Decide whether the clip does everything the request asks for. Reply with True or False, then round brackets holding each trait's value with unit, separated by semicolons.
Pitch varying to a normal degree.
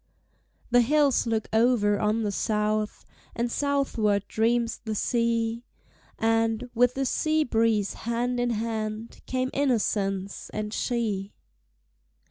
False (2.3 semitones)